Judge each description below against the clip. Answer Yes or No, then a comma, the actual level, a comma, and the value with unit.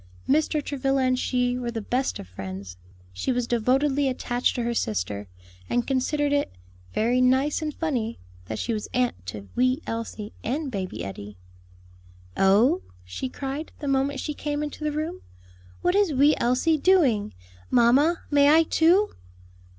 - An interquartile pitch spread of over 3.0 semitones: Yes, average, 4.5 semitones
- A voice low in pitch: No, very high, 255 Hz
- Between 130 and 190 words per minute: Yes, average, 160 wpm